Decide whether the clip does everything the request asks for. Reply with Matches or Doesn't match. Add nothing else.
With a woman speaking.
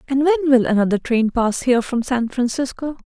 Matches